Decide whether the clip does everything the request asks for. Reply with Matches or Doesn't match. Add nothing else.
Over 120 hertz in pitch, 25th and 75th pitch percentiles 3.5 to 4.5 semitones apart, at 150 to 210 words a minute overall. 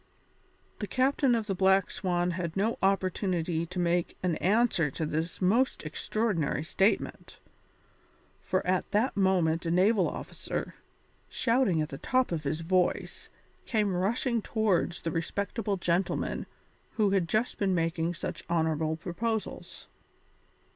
Doesn't match